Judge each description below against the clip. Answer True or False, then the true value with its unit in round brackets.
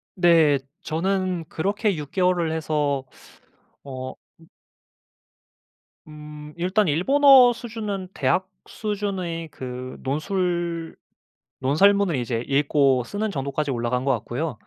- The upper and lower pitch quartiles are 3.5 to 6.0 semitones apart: True (5.4 semitones)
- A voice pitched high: False (165 Hz)